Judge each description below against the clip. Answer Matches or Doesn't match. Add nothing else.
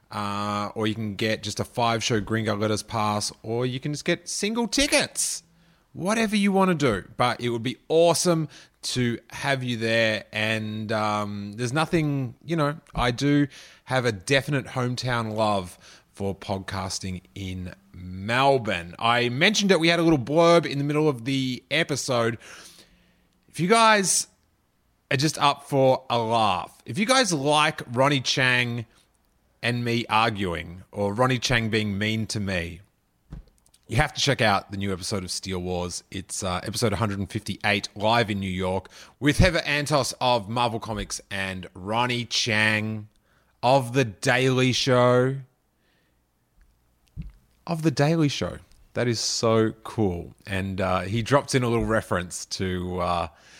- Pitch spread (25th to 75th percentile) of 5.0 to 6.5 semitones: Matches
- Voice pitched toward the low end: Matches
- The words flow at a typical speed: Matches